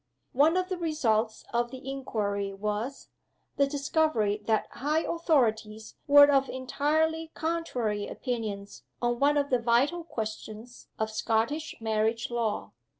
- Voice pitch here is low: No, high, 245 Hz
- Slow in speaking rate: Yes, slow, 130 wpm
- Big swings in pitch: No, average, 5.0 semitones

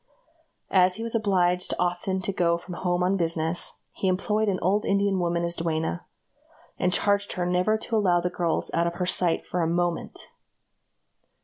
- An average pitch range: No, narrow, 2.2 semitones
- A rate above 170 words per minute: Yes, average, 180 wpm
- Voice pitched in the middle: Yes, medium, 180 Hz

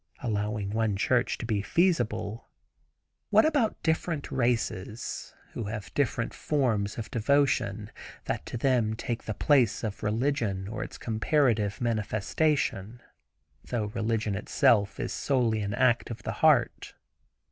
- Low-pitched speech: Yes, low, 115 Hz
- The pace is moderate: No, slow, 130 wpm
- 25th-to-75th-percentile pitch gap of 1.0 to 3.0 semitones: No, average, 3.4 semitones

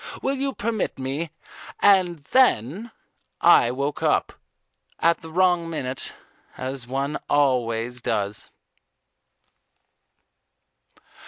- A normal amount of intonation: No, wide, 6.2 semitones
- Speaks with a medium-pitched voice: Yes, medium, 145 Hz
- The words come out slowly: Yes, slow, 95 wpm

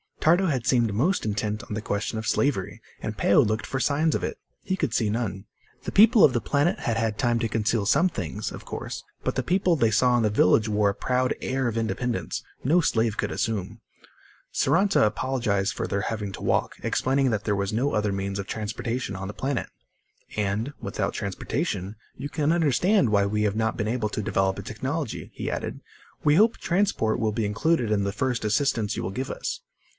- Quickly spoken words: Yes, fast, 210 wpm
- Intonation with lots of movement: No, average, 4.7 semitones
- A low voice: Yes, low, 115 Hz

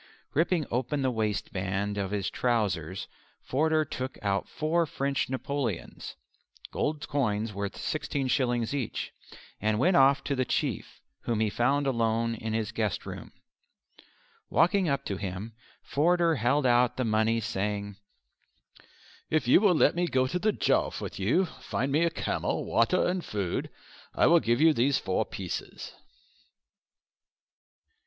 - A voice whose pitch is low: Yes, low, 125 Hz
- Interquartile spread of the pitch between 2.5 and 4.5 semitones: No, wide, 5.6 semitones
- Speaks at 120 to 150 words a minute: Yes, average, 140 wpm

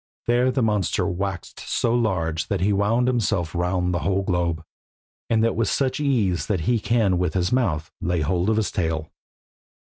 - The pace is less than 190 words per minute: Yes, average, 180 wpm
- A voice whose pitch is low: Yes, very low, 95 Hz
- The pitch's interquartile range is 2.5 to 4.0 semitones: No, average, 4.7 semitones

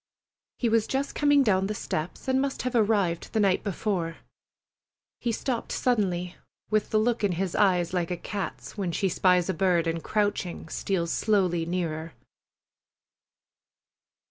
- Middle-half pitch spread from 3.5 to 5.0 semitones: Yes, average, 3.9 semitones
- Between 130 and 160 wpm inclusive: Yes, average, 150 wpm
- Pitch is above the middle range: Yes, high, 195 Hz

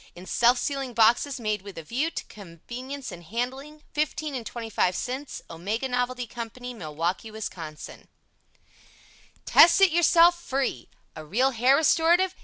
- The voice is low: No, high, 245 Hz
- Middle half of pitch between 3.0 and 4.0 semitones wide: No, average, 4.9 semitones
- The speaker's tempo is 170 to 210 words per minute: No, average, 140 wpm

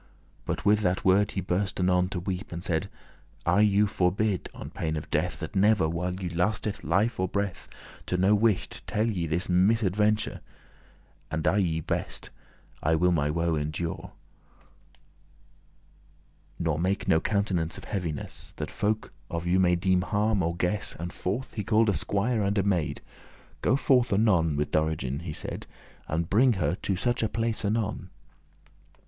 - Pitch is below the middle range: Yes, very low, 95 Hz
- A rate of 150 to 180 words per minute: Yes, average, 165 wpm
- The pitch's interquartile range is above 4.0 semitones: No, average, 3.6 semitones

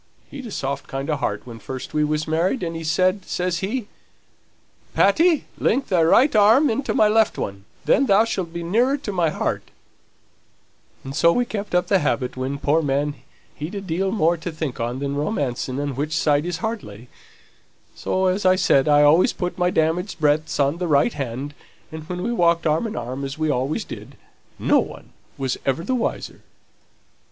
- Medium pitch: Yes, medium, 165 Hz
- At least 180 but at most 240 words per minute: Yes, average, 195 wpm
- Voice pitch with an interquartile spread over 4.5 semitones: Yes, wide, 5.6 semitones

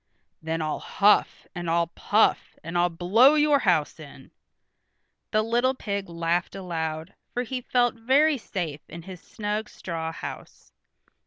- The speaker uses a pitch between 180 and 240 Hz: Yes, high, 190 Hz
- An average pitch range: No, wide, 6.0 semitones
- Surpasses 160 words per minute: No, average, 145 wpm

